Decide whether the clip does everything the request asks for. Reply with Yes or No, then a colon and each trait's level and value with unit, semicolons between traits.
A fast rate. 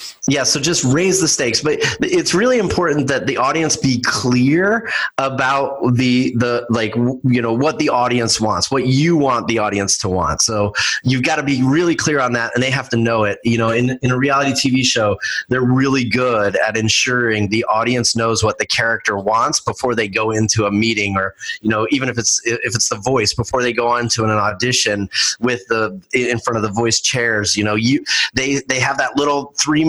Yes: fast, 215 wpm